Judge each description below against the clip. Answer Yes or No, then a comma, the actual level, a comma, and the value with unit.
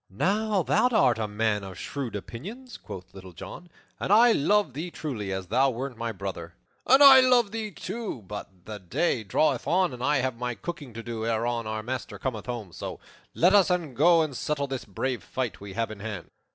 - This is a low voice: Yes, low, 125 Hz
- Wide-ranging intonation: Yes, wide, 8.4 semitones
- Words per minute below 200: No, fast, 205 wpm